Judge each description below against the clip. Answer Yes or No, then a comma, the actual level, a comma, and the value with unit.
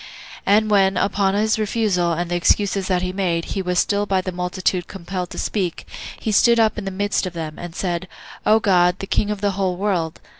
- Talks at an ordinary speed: No, fast, 220 wpm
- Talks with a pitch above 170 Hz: Yes, high, 190 Hz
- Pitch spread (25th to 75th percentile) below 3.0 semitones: Yes, narrow, 2.4 semitones